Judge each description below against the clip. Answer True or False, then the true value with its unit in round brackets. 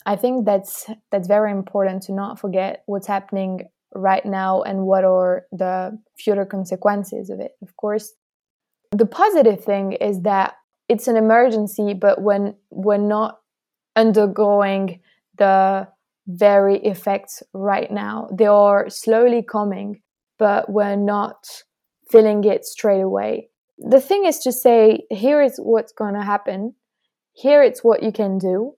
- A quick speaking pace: False (145 wpm)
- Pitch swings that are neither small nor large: False (2.2 semitones)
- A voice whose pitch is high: True (205 Hz)